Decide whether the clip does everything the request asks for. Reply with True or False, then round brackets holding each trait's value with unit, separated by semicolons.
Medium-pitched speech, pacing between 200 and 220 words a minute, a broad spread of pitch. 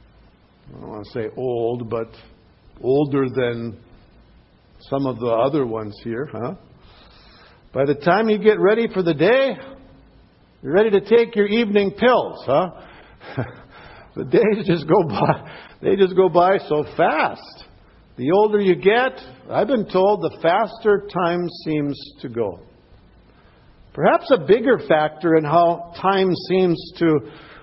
False (170 Hz; 145 wpm; 6.5 semitones)